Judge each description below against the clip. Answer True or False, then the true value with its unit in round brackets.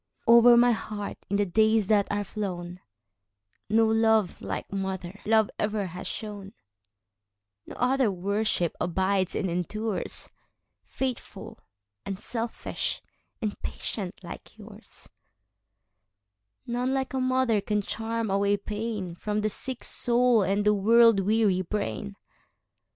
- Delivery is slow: True (105 wpm)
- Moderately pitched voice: False (205 Hz)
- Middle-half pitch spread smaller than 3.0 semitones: False (3.8 semitones)